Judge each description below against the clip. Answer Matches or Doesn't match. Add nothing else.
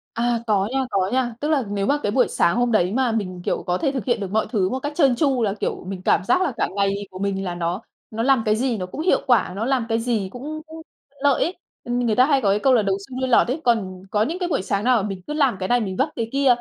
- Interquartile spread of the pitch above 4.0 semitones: Matches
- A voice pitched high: Matches